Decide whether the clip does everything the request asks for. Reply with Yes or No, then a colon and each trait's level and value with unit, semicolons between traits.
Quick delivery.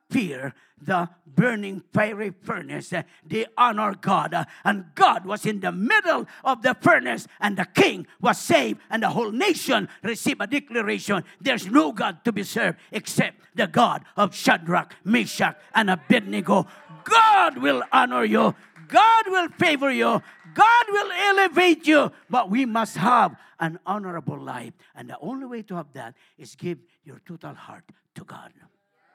No: average, 155 wpm